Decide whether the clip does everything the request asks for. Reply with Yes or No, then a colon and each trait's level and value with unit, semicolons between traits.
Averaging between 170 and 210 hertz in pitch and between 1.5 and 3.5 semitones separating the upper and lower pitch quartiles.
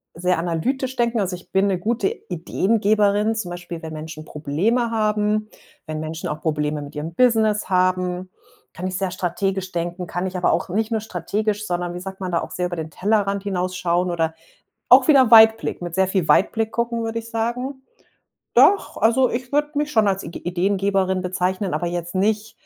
No: high, 190 Hz; average, 3.9 semitones